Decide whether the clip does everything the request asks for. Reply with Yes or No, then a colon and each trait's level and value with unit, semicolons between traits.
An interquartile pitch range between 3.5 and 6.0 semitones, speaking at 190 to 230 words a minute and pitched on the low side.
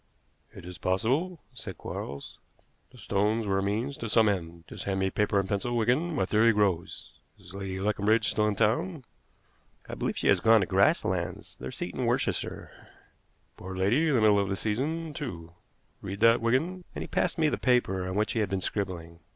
Yes: average, 4.1 semitones; average, 200 wpm; low, 105 Hz